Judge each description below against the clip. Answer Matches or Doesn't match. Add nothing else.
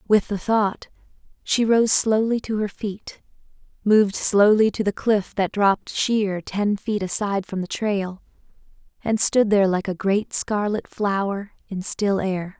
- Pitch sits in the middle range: Doesn't match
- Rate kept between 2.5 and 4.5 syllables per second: Matches